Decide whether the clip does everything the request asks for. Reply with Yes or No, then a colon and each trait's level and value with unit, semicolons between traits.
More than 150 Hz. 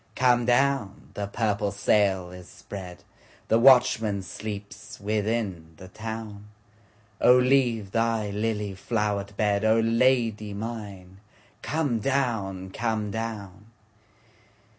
No: low, 105 Hz